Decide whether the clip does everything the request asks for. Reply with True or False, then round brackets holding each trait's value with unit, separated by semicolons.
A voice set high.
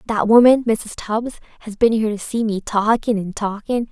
True (220 Hz)